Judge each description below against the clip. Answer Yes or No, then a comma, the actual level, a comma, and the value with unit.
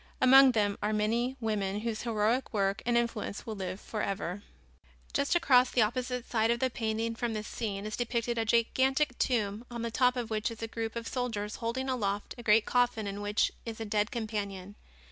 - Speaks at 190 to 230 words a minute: Yes, average, 200 wpm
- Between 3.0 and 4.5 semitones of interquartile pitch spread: No, narrow, 2.5 semitones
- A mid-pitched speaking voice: No, high, 225 Hz